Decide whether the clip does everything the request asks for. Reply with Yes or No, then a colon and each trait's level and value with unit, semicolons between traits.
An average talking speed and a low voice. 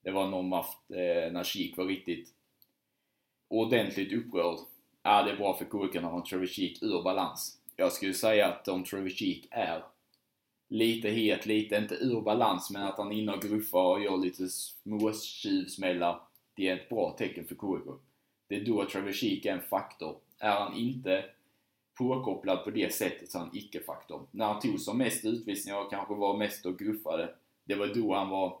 Yes: average, 180 wpm; low, 100 Hz